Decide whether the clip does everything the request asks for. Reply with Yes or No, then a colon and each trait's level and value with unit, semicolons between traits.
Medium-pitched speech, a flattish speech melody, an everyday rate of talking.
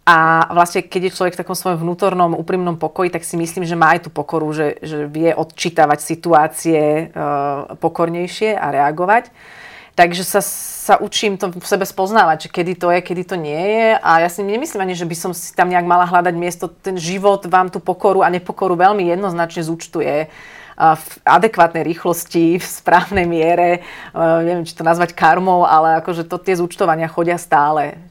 No: medium, 175 Hz; narrow, 2.2 semitones; fast, 180 wpm